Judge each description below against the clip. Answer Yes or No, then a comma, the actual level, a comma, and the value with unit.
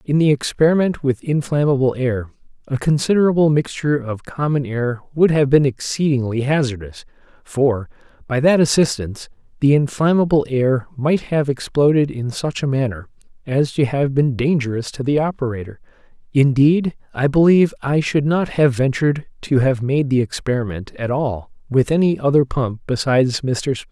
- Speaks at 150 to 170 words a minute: Yes, average, 155 wpm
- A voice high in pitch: No, low, 135 Hz